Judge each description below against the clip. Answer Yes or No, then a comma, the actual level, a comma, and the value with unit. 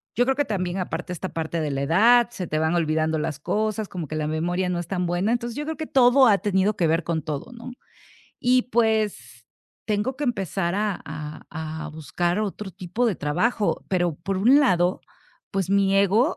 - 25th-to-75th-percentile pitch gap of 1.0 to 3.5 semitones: No, average, 5.2 semitones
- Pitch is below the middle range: No, high, 190 Hz